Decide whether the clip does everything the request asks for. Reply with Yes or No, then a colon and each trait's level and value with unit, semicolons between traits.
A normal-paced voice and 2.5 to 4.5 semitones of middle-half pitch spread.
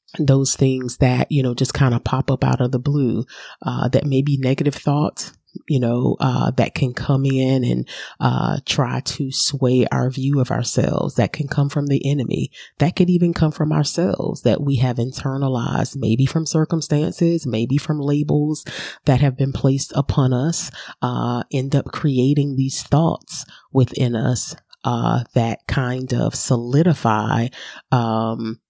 Yes: average, 165 wpm; average, 2.8 semitones